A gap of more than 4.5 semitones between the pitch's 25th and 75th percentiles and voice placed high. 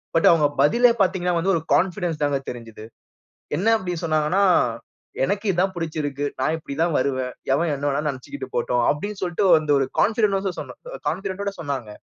No: average, 5.0 semitones; medium, 160 Hz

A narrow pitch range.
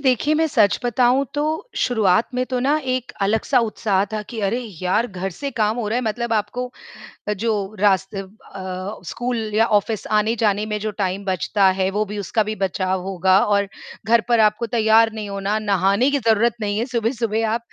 No: average, 3.0 semitones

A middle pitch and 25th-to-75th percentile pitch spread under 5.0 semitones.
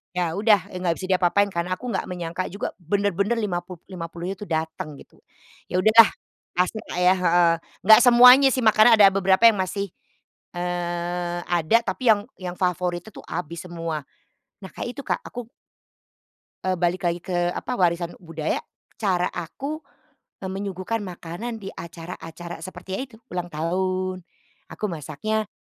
Yes: medium, 180 Hz; average, 2.8 semitones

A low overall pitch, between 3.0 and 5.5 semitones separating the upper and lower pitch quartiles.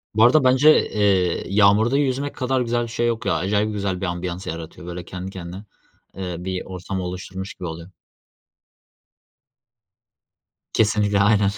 Yes: low, 100 Hz; average, 3.8 semitones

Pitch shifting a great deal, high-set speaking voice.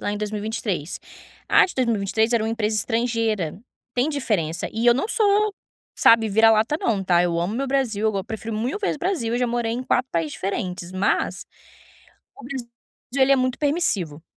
No: average, 4.2 semitones; high, 225 Hz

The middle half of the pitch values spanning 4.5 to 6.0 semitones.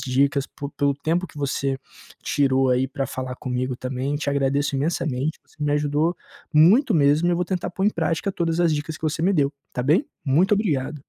No: average, 3.7 semitones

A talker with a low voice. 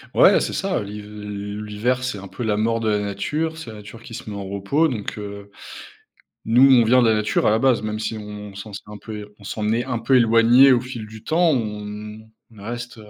Yes: low, 110 Hz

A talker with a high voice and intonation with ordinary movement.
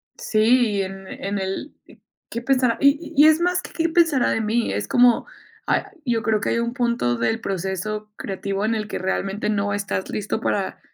Yes: high, 220 Hz; average, 3.9 semitones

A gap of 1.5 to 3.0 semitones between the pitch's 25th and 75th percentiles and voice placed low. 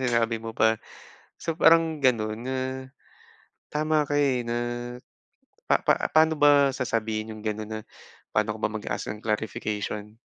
No: average, 4.9 semitones; low, 115 Hz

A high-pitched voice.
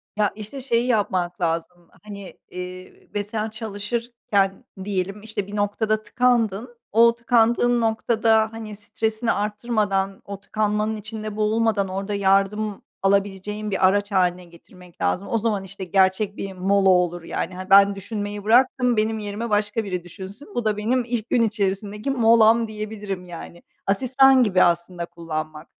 Yes: high, 205 Hz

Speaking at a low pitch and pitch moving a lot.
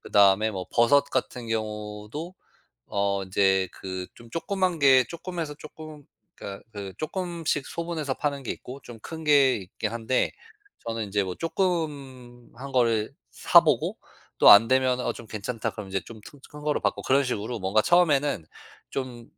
Yes: low, 125 Hz; wide, 5.7 semitones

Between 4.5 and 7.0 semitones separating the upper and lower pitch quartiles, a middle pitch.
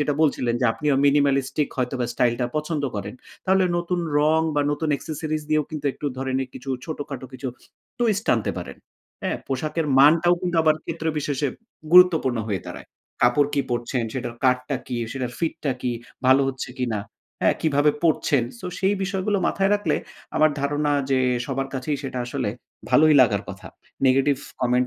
No: average, 3.5 semitones; medium, 145 Hz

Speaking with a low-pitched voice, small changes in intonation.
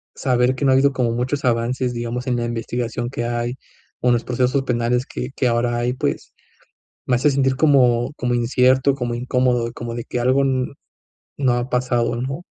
Yes: low, 125 Hz; narrow, 1.6 semitones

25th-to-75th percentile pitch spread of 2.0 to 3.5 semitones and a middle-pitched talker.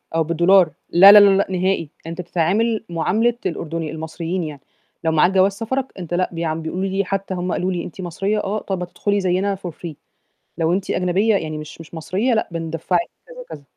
Yes: average, 3.1 semitones; medium, 180 Hz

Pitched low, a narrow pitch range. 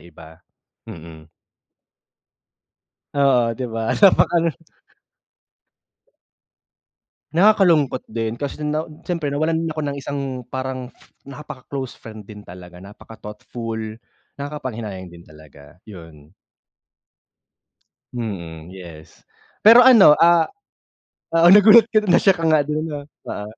No: low, 130 Hz; wide, 8.1 semitones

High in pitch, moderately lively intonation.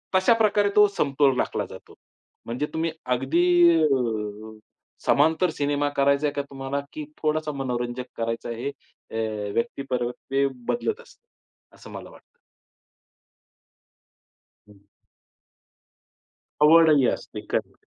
No: medium, 140 Hz; average, 4.5 semitones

